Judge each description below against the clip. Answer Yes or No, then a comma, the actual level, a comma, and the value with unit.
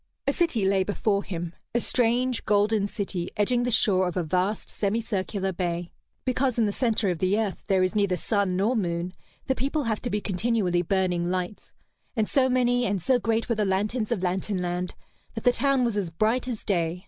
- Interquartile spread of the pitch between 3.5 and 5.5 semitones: Yes, average, 4.1 semitones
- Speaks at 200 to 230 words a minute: Yes, fast, 205 wpm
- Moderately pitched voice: No, high, 205 Hz